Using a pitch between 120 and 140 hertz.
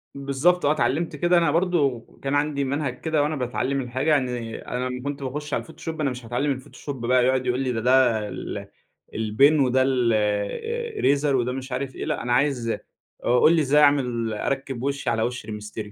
Yes: low, 135 Hz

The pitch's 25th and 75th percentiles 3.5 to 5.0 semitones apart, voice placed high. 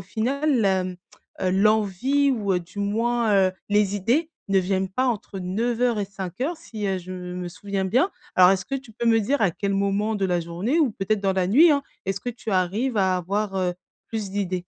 Yes: average, 3.8 semitones; high, 200 Hz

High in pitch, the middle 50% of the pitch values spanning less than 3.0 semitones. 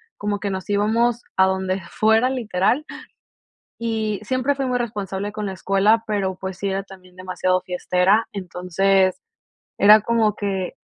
Yes: high, 200 Hz; narrow, 2.6 semitones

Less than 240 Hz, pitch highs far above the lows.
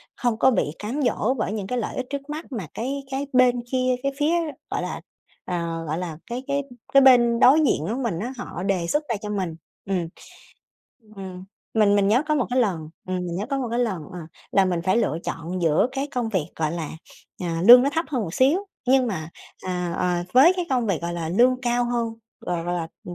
Yes: high, 225 Hz; wide, 6.3 semitones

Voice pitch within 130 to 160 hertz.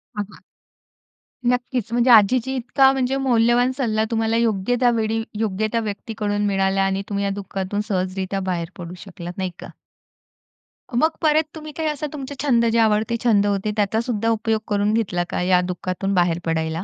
No: high, 215 Hz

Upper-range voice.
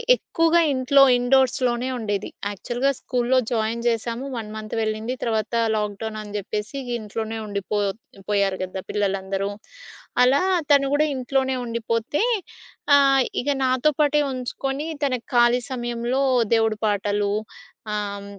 Yes: high, 235 Hz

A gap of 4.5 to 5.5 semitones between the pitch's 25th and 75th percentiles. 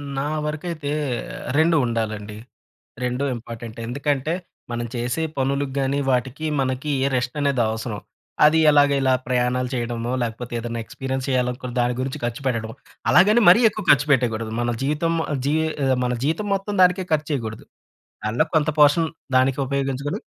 No: average, 3.6 semitones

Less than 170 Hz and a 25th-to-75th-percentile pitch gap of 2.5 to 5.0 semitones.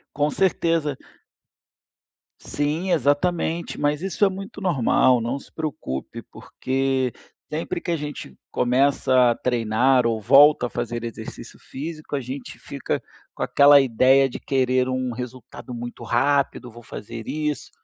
Yes: low, 135 Hz; average, 3.5 semitones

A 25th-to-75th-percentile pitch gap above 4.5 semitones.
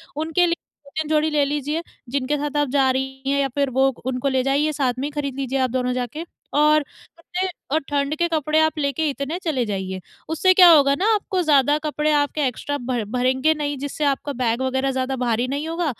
No: average, 2.8 semitones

